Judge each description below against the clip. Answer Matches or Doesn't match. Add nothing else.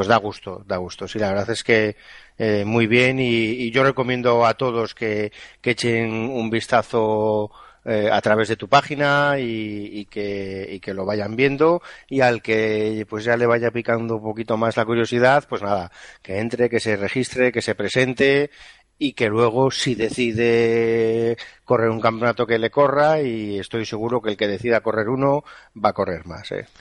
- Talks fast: Matches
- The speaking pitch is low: Matches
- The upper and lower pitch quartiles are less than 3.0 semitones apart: Matches